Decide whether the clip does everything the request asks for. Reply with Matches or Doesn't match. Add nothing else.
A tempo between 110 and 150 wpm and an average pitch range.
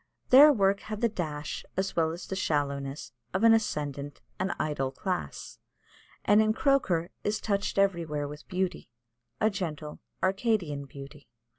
Doesn't match